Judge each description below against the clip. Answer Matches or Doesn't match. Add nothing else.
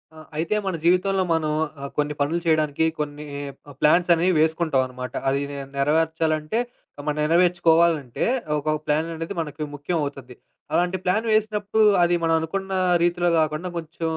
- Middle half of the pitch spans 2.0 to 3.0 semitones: Matches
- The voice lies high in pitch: Doesn't match